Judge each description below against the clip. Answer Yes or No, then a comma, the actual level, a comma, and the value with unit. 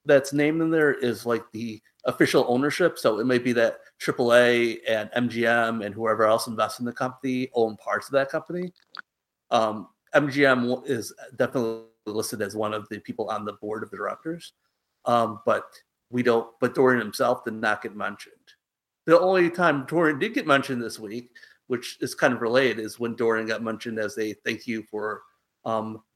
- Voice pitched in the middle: No, low, 115 Hz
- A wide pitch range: No, average, 2.9 semitones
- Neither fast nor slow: Yes, average, 185 wpm